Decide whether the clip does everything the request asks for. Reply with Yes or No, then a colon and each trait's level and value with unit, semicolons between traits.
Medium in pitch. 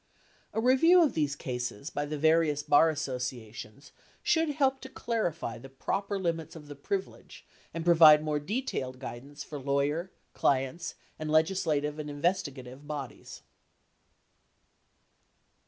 Yes: medium, 150 Hz